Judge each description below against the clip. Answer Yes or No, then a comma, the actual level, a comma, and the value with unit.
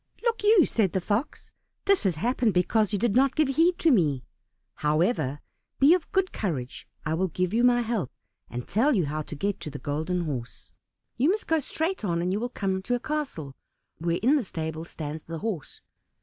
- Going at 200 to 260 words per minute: Yes, fast, 205 wpm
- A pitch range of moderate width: No, wide, 8.7 semitones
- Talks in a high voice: Yes, high, 200 Hz